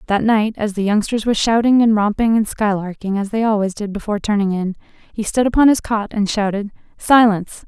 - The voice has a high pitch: Yes, high, 210 Hz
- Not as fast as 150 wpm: No, fast, 205 wpm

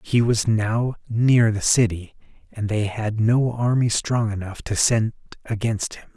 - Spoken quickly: No, average, 165 wpm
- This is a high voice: No, low, 110 Hz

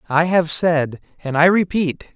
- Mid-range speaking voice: Yes, medium, 165 Hz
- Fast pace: No, average, 165 wpm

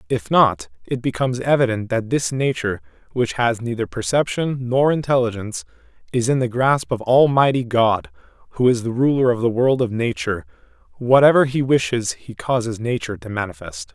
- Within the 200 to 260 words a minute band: No, average, 165 wpm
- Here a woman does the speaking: No, male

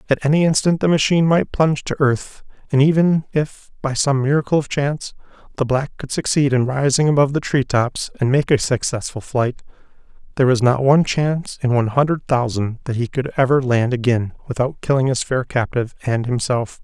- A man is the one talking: Yes, male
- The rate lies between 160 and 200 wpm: Yes, average, 190 wpm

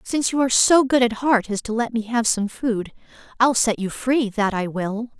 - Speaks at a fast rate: Yes, fast, 240 wpm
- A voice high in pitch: Yes, high, 230 Hz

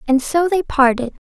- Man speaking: No, female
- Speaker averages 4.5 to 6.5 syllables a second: Yes, 5.1 syllables/s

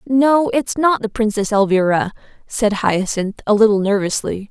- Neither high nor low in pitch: No, high, 225 Hz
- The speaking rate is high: No, average, 145 wpm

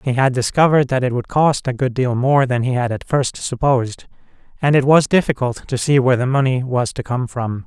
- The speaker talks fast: Yes, fast, 235 wpm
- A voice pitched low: Yes, low, 130 Hz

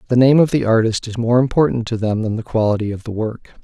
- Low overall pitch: Yes, low, 115 Hz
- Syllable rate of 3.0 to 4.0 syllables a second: No, 6.3 syllables/s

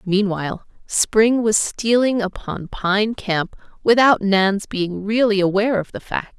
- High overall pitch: Yes, high, 210 Hz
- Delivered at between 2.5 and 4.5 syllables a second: Yes, 4.0 syllables/s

